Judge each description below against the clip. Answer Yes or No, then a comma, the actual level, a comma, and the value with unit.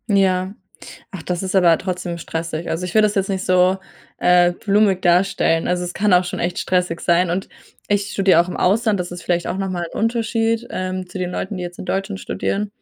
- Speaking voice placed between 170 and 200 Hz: Yes, medium, 185 Hz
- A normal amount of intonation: No, narrow, 1.9 semitones